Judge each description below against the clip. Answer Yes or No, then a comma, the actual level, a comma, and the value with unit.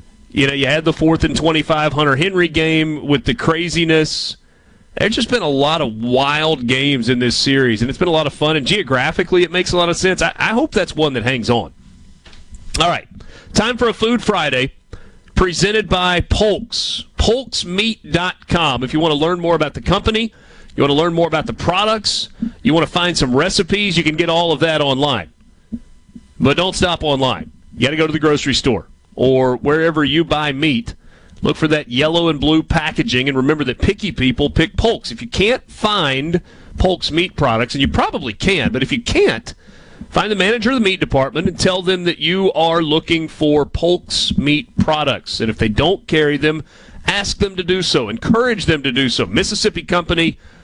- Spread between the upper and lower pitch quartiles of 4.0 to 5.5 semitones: Yes, average, 4.5 semitones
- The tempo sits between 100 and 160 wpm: No, fast, 205 wpm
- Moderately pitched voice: Yes, medium, 160 Hz